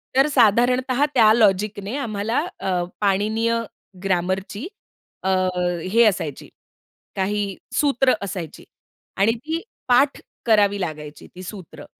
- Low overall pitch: No, high, 210 Hz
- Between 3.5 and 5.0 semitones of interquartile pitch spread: Yes, average, 4.2 semitones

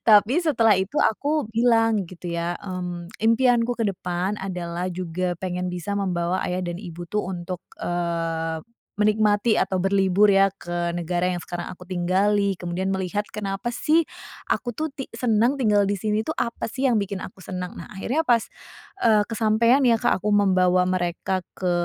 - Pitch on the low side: No, high, 195 Hz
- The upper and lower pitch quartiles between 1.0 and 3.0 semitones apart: No, average, 3.7 semitones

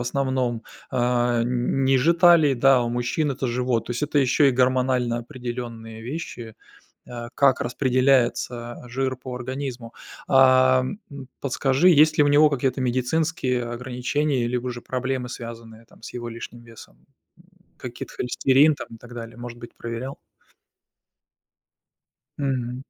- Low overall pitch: Yes, low, 125 Hz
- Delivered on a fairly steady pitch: Yes, narrow, 2.0 semitones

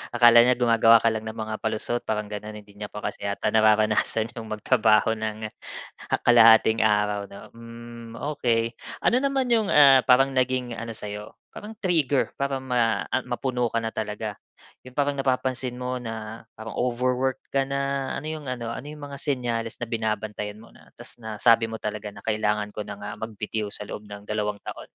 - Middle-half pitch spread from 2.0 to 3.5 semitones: Yes, average, 3.0 semitones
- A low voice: Yes, low, 115 Hz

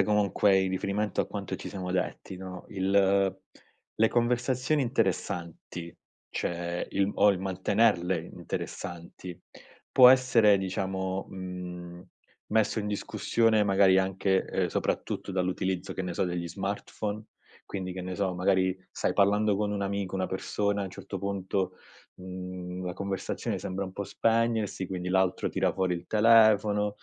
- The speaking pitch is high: No, very low, 95 Hz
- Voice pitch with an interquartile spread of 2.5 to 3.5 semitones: No, narrow, 2.0 semitones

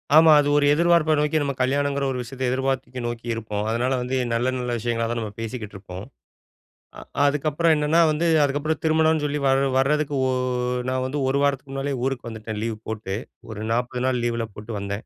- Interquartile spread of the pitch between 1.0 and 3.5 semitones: No, average, 4.0 semitones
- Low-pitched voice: Yes, low, 130 Hz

